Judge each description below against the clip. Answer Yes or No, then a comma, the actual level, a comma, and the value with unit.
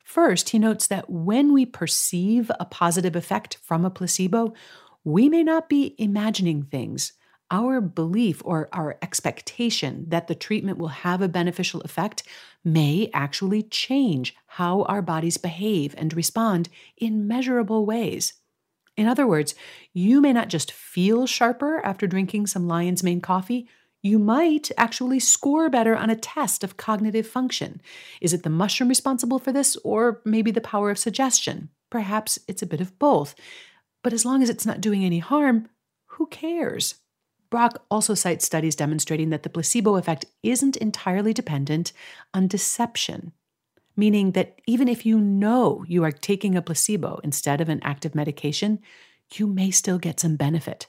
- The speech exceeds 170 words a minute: No, average, 160 wpm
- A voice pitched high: Yes, high, 205 Hz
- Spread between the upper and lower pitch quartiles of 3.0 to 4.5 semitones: No, wide, 5.6 semitones